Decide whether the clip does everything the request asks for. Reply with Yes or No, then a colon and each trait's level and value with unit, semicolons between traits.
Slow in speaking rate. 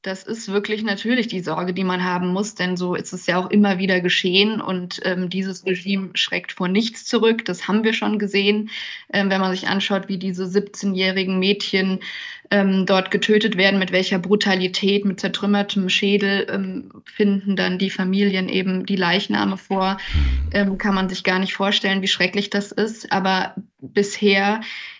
No: average, 175 wpm